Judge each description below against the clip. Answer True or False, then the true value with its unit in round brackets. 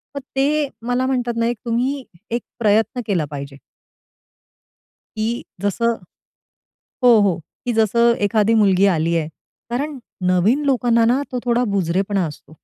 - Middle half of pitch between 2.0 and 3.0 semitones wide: False (4.1 semitones)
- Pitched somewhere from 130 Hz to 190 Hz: False (230 Hz)